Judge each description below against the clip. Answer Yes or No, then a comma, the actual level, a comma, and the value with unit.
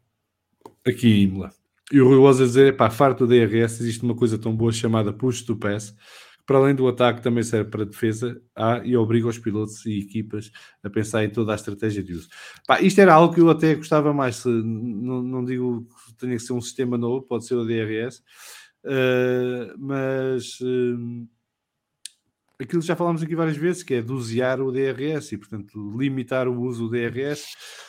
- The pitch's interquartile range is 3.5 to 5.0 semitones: No, average, 2.8 semitones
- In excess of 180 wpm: Yes, average, 200 wpm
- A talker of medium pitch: No, low, 120 Hz